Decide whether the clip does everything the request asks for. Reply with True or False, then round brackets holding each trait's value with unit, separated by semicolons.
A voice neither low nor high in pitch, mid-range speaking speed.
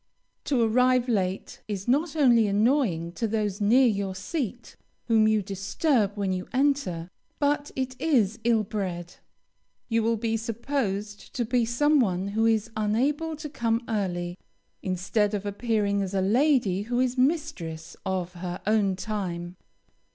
False (220 Hz; 150 wpm)